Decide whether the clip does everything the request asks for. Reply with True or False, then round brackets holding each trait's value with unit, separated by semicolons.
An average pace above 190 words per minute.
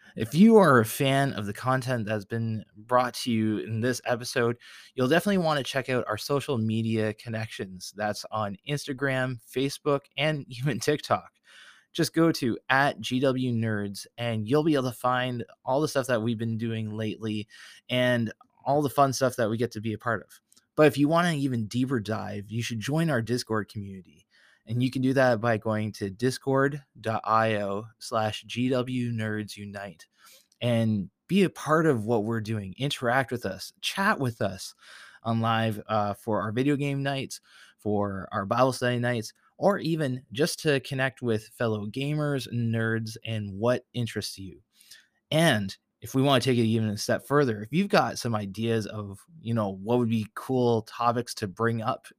False (180 wpm)